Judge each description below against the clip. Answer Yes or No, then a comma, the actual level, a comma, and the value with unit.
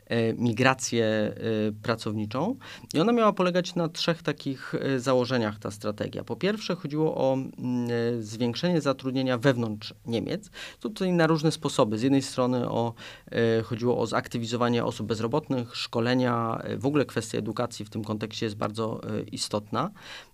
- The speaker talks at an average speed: Yes, average, 130 wpm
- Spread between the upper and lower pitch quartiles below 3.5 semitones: No, average, 4.1 semitones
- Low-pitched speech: Yes, low, 120 Hz